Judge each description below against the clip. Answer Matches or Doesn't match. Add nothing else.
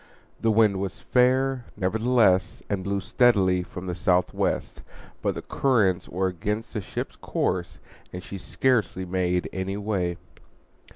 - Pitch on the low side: Matches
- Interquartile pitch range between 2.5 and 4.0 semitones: Matches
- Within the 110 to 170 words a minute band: Matches